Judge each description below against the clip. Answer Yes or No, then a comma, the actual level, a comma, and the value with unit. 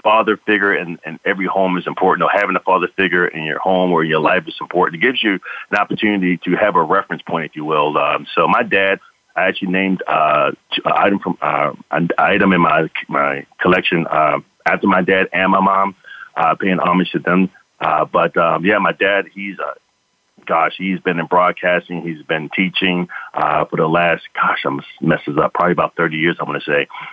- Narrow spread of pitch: Yes, narrow, 1.4 semitones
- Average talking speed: No, fast, 210 wpm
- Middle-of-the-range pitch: No, very low, 95 Hz